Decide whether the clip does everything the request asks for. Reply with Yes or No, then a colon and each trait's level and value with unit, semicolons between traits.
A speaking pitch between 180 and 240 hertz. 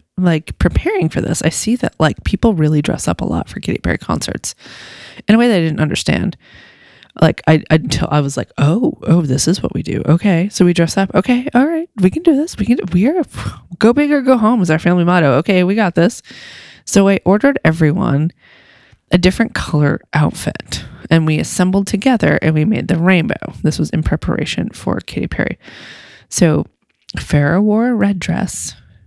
Yes: medium, 185 Hz